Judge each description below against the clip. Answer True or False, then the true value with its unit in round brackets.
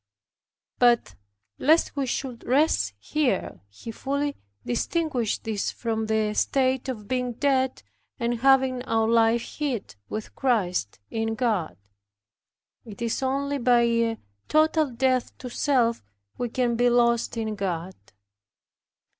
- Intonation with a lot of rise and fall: False (3.0 semitones)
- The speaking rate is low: True (125 wpm)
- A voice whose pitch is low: False (240 Hz)